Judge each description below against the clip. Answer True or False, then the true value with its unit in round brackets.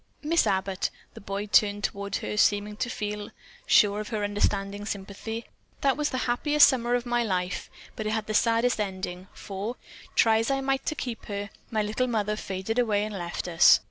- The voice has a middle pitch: False (210 Hz)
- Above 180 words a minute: True (195 wpm)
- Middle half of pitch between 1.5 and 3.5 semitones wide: True (3.0 semitones)